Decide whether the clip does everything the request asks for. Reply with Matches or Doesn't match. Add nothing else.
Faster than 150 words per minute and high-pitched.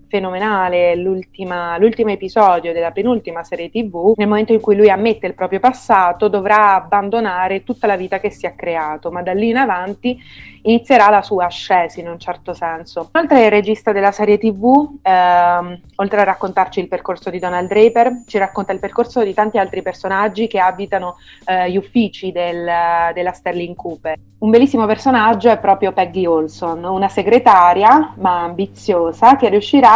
Matches